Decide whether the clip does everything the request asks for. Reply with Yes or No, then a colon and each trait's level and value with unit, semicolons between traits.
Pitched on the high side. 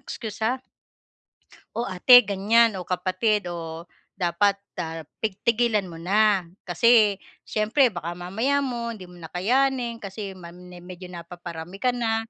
Yes: high, 200 Hz